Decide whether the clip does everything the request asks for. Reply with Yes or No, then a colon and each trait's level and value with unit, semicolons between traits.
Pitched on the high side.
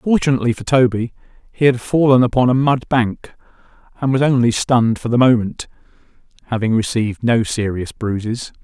No: low, 120 Hz